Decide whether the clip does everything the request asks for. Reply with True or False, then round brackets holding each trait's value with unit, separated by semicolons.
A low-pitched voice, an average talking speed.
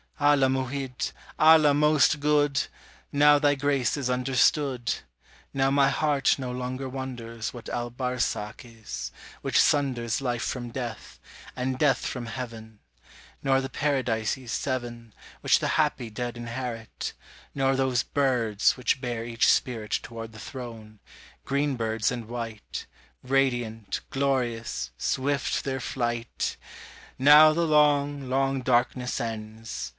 False (125 Hz; 125 wpm)